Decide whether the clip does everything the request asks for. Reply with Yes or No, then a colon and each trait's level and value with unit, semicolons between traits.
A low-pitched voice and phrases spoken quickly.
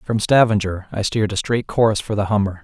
Yes: low, 105 Hz; fast, 230 wpm